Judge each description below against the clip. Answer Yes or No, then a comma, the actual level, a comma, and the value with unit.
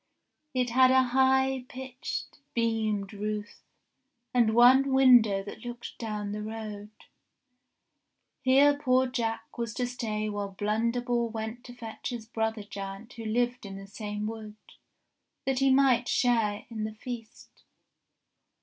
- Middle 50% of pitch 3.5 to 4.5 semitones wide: No, average, 2.9 semitones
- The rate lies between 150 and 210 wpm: No, slow, 135 wpm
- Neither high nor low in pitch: No, high, 230 Hz